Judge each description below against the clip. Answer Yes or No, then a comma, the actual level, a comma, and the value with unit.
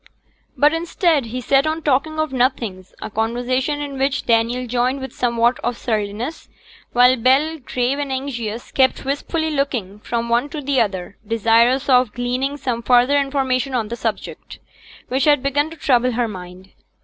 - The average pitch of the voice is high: Yes, very high, 255 Hz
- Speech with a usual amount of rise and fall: Yes, average, 3.1 semitones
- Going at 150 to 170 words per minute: Yes, average, 165 wpm